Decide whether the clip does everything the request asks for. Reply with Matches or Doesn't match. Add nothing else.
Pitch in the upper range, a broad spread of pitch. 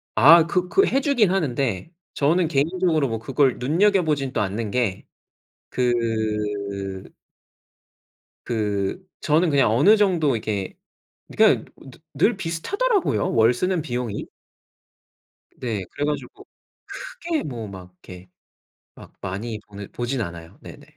Doesn't match